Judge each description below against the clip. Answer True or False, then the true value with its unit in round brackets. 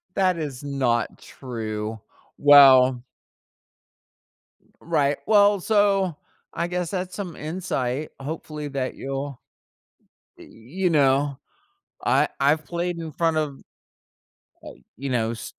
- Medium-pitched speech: True (145 Hz)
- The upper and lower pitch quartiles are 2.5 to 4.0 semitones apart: False (4.6 semitones)